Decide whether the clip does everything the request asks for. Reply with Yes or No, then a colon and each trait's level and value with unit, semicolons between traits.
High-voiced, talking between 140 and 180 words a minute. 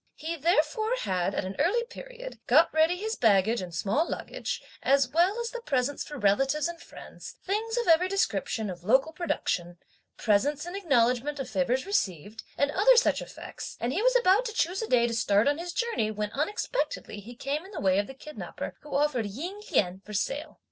No: very high, 290 Hz; average, 200 wpm